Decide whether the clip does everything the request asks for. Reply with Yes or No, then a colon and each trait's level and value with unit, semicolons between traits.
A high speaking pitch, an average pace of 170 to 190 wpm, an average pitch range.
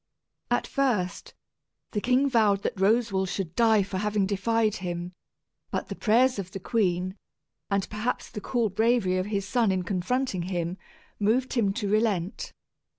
No: high, 205 Hz; average, 155 wpm; average, 3.6 semitones